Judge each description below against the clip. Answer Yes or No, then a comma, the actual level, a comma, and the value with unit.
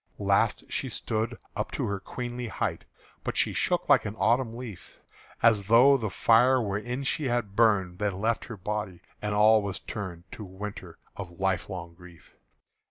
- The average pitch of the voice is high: No, low, 105 Hz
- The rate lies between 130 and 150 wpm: No, average, 165 wpm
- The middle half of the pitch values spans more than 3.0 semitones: Yes, average, 3.5 semitones